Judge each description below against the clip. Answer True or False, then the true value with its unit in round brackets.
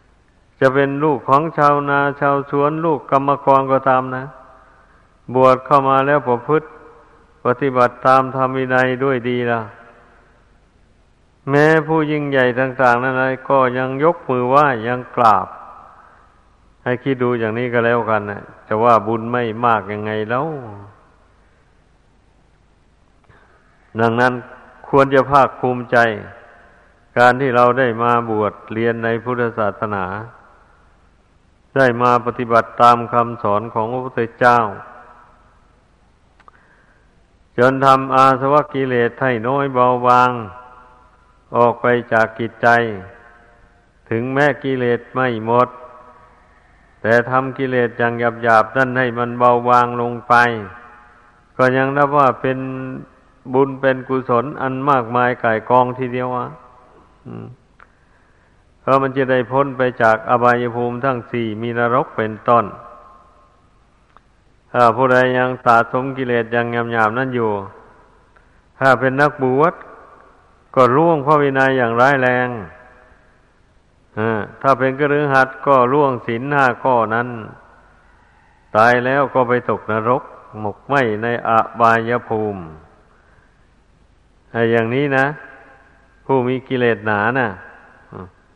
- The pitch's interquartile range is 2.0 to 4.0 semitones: True (2.4 semitones)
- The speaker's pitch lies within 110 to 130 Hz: True (125 Hz)